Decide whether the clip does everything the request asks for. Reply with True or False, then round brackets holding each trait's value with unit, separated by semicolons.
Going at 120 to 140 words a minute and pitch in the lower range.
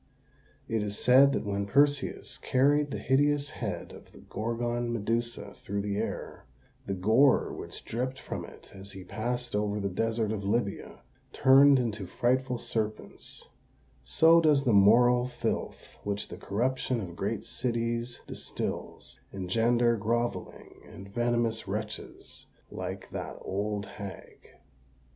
True (135 wpm; 115 Hz)